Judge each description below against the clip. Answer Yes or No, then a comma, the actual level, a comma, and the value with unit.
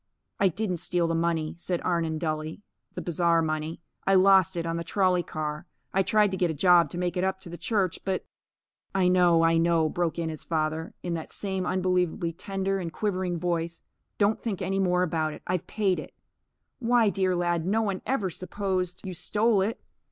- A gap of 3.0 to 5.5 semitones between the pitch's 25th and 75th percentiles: No, narrow, 2.5 semitones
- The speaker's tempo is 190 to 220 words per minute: Yes, fast, 205 wpm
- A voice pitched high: No, medium, 180 Hz